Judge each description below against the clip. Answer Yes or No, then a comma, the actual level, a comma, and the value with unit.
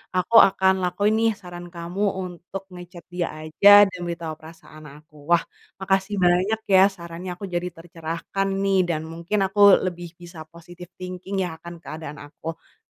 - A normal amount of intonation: No, narrow, 2.2 semitones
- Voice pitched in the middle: Yes, medium, 175 Hz